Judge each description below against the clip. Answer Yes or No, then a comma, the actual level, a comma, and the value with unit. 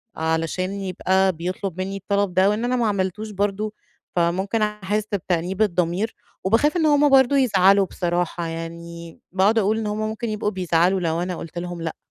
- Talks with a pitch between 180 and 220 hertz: Yes, high, 190 Hz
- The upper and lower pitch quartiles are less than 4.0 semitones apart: Yes, average, 3.4 semitones